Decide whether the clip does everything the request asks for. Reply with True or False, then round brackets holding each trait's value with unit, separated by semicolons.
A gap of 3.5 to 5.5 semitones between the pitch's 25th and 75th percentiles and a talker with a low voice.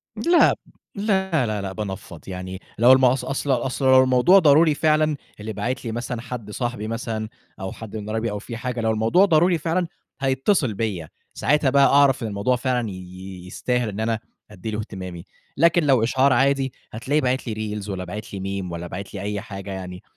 True (4.7 semitones; 115 Hz)